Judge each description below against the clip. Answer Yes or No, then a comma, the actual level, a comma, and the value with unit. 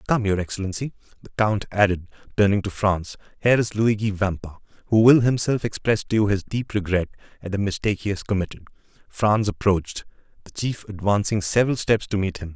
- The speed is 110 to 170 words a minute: No, average, 180 wpm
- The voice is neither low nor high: No, low, 100 Hz